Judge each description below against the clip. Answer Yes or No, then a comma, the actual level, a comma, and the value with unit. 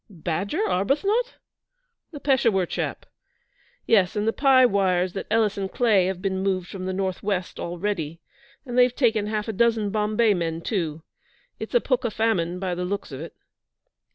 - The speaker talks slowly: No, average, 165 wpm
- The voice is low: No, high, 200 Hz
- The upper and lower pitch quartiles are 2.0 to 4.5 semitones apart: Yes, average, 3.9 semitones